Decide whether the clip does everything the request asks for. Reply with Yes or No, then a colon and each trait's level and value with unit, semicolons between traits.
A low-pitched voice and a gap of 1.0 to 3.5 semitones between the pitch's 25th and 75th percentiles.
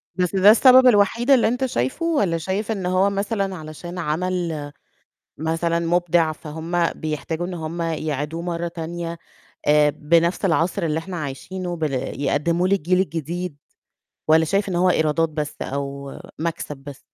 No: medium, 170 Hz; average, 2.9 semitones